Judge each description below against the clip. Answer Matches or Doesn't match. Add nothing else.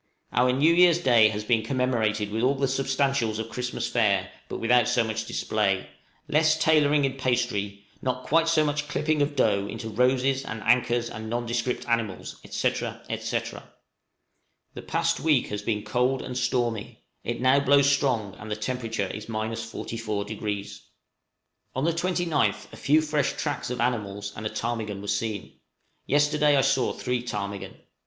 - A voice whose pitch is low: Matches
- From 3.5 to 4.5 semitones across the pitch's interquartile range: Matches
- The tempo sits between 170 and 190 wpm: Doesn't match